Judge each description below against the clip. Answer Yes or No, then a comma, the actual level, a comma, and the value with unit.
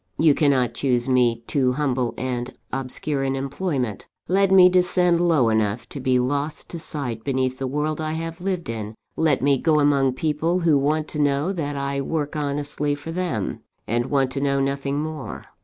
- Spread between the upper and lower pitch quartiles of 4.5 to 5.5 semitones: No, average, 3.3 semitones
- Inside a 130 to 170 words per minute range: No, average, 185 wpm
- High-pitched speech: No, medium, 140 Hz